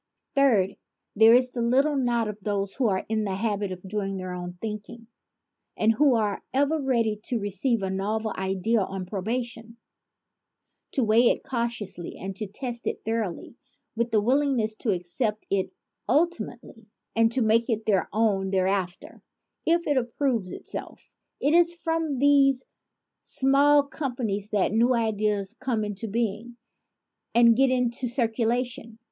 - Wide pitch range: No, average, 3.8 semitones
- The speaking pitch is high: Yes, high, 225 Hz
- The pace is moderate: Yes, average, 150 wpm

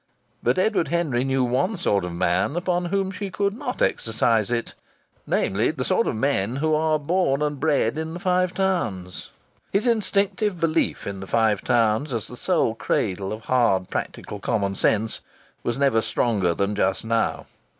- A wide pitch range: Yes, wide, 8.3 semitones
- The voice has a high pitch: No, low, 130 Hz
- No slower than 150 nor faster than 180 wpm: Yes, average, 170 wpm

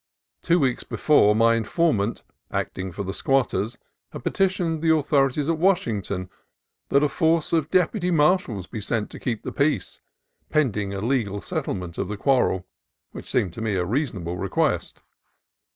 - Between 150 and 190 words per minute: Yes, average, 160 wpm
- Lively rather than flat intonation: Yes, wide, 7.7 semitones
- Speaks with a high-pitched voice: No, low, 125 Hz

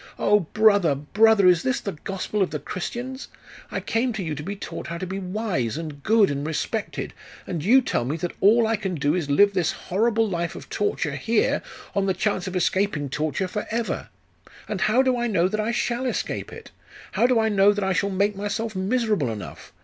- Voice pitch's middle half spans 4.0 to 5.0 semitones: Yes, average, 4.5 semitones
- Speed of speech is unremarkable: No, fast, 215 wpm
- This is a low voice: No, high, 200 Hz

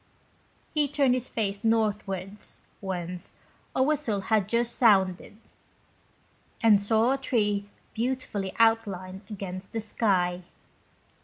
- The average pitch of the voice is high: Yes, high, 210 Hz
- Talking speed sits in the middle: No, slow, 105 wpm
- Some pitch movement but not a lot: Yes, average, 3.2 semitones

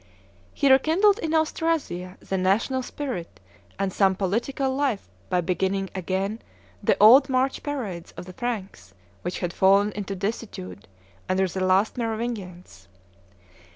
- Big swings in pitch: Yes, wide, 5.8 semitones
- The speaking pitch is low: No, high, 200 Hz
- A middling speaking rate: No, slow, 130 wpm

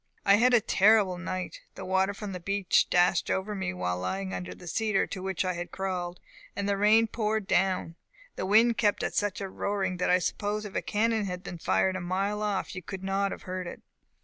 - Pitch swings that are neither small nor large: No, narrow, 2.3 semitones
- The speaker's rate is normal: No, fast, 225 wpm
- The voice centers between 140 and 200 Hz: Yes, high, 190 Hz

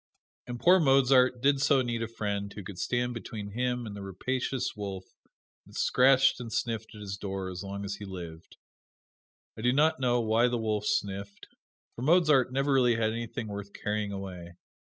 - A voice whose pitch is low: Yes, low, 115 Hz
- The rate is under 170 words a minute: No, average, 185 wpm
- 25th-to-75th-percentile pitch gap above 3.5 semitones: Yes, average, 3.9 semitones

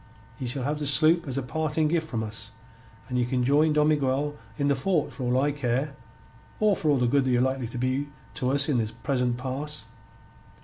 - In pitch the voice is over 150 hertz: No, medium, 140 Hz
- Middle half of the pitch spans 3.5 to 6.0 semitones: No, average, 3.0 semitones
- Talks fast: Yes, fast, 220 wpm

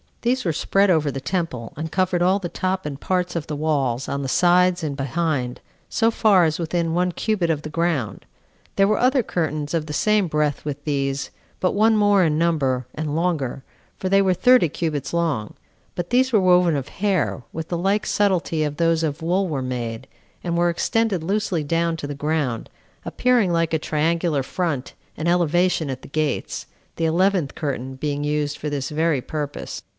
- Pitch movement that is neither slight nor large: Yes, average, 3.9 semitones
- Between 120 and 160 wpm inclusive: No, average, 190 wpm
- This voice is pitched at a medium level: Yes, medium, 165 Hz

